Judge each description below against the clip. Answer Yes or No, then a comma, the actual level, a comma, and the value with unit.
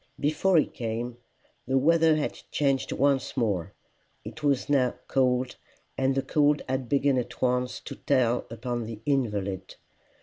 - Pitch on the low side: Yes, low, 130 Hz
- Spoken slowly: No, average, 145 wpm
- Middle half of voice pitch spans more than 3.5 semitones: No, average, 2.9 semitones